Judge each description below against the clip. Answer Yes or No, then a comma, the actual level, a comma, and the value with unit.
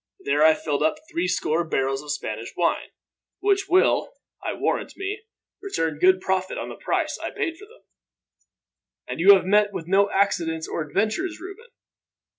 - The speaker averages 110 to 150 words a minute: No, average, 175 wpm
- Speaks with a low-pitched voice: No, high, 190 Hz